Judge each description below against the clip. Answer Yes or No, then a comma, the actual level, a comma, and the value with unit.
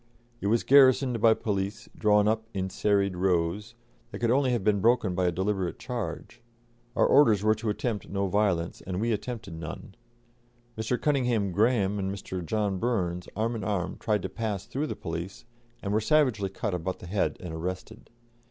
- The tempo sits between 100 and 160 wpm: No, average, 180 wpm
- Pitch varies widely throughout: No, average, 3.6 semitones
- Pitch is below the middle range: Yes, low, 105 Hz